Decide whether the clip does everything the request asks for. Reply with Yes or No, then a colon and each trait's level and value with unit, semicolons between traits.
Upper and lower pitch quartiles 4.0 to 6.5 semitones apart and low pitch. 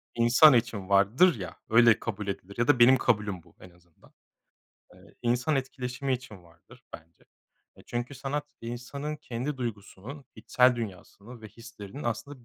Yes: average, 4.3 semitones; low, 120 Hz